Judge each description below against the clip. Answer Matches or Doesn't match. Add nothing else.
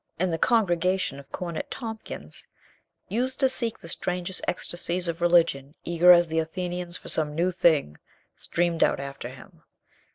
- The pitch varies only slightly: Matches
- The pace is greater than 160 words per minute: Doesn't match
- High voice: Doesn't match